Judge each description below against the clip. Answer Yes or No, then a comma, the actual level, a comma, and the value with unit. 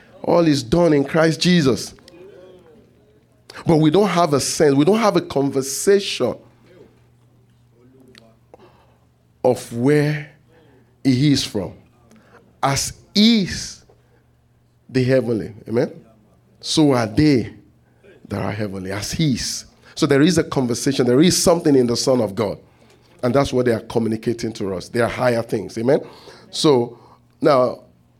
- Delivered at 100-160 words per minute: Yes, slow, 135 wpm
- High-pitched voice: No, low, 125 Hz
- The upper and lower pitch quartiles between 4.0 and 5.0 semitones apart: Yes, average, 4.7 semitones